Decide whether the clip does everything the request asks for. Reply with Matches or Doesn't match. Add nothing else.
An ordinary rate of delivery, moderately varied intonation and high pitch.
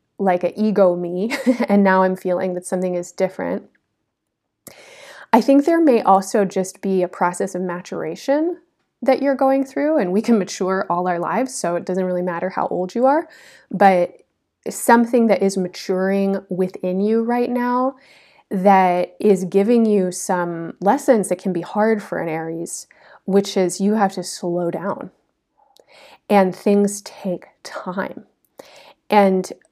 Matches